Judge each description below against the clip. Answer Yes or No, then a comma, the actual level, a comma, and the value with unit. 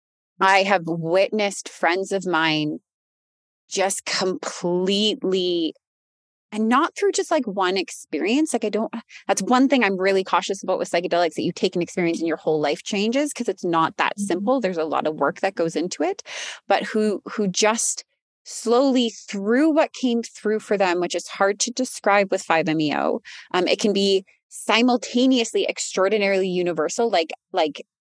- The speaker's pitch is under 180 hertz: No, high, 195 Hz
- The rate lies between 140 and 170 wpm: Yes, average, 165 wpm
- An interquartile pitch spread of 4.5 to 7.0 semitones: Yes, average, 4.9 semitones